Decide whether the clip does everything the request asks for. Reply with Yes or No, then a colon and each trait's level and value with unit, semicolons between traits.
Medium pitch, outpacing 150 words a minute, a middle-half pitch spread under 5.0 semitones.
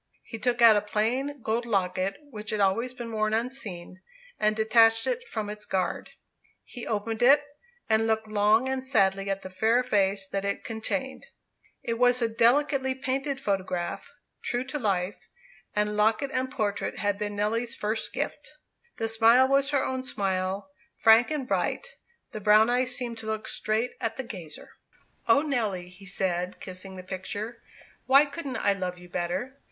No: high, 220 Hz; average, 170 wpm; average, 3.9 semitones